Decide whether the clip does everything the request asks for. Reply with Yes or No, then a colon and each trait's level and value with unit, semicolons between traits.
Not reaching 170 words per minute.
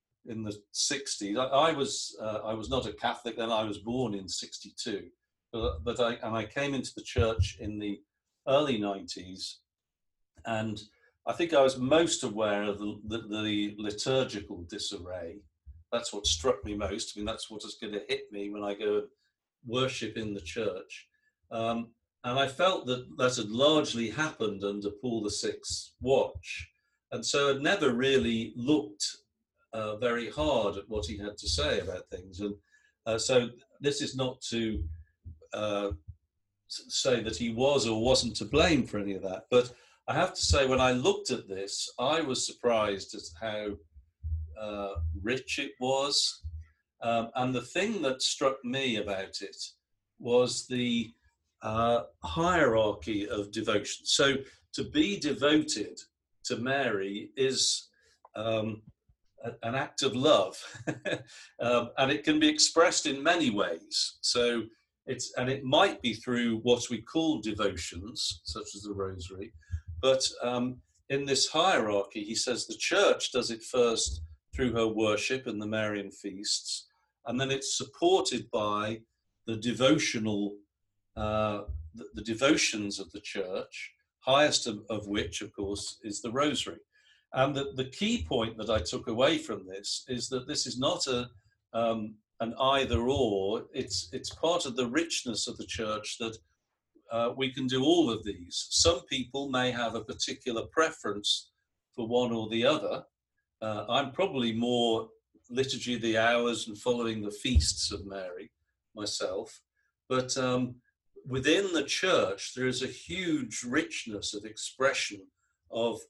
Yes: average, 155 wpm